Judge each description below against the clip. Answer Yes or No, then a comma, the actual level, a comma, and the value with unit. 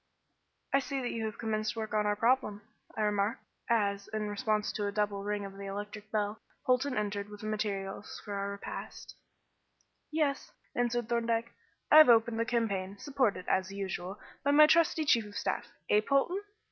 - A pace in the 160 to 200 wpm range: Yes, average, 175 wpm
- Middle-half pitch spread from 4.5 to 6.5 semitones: No, average, 2.8 semitones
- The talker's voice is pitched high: Yes, high, 215 Hz